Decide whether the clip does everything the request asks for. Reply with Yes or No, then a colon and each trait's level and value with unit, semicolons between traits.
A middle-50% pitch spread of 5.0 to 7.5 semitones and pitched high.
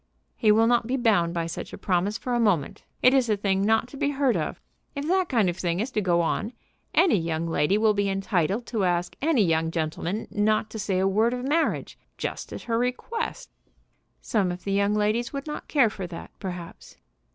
Yes: average, 5.3 semitones; high, 210 Hz